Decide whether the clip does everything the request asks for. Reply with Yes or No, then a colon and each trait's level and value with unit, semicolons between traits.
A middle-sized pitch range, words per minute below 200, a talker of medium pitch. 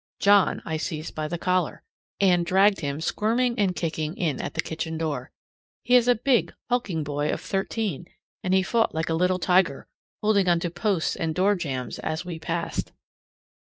Yes: average, 4.0 semitones; average, 180 wpm; medium, 175 Hz